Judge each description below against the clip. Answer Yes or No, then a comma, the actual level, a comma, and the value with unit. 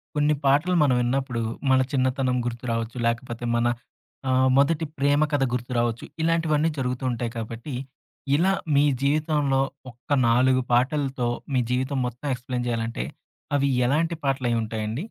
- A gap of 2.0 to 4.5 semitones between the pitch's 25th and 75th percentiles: Yes, average, 3.1 semitones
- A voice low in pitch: Yes, low, 130 Hz